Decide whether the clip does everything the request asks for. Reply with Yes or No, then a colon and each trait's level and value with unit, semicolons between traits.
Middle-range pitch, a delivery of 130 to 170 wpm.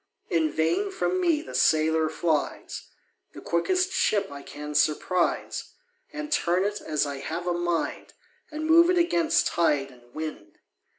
Yes: medium, 170 Hz; average, 155 wpm